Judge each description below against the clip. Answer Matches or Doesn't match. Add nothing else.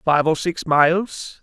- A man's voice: Matches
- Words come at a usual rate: Matches